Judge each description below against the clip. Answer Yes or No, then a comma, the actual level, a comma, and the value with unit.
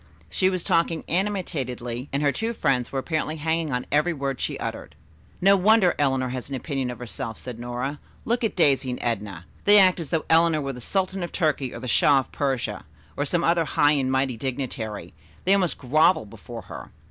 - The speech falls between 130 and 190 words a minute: No, fast, 205 wpm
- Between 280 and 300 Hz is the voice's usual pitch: No, medium, 145 Hz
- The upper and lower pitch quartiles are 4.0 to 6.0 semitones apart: Yes, average, 5.1 semitones